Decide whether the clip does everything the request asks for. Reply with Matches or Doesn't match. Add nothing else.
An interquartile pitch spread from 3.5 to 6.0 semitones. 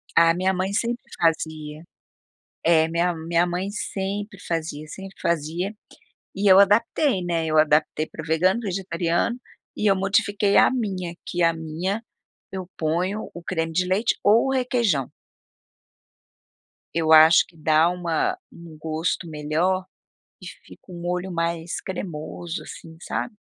Doesn't match